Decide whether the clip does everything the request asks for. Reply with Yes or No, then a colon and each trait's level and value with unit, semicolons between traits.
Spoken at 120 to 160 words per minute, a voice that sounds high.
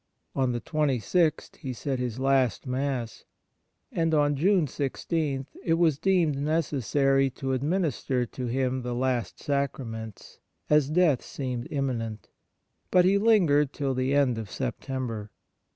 No: slow, 135 wpm; low, 135 Hz